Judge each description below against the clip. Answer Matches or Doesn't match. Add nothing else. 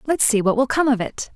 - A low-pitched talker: Doesn't match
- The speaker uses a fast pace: Matches